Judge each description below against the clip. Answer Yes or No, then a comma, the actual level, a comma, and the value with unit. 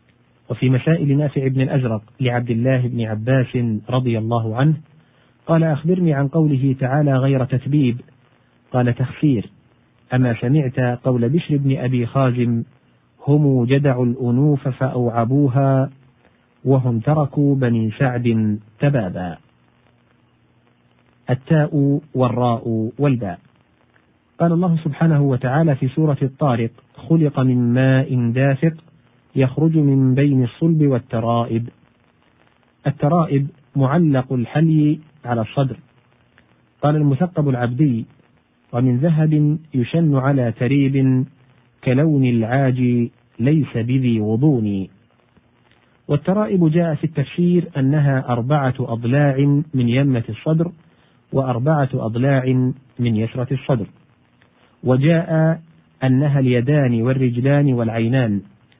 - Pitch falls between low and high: No, low, 130 Hz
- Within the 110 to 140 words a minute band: No, average, 95 wpm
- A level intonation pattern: No, average, 3.2 semitones